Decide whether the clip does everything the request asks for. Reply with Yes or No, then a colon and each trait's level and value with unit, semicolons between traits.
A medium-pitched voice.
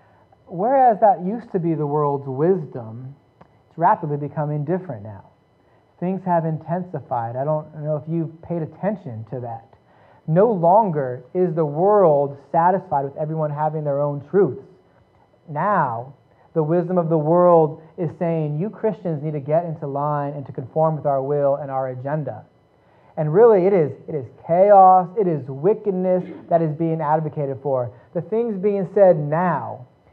Yes: medium, 155 Hz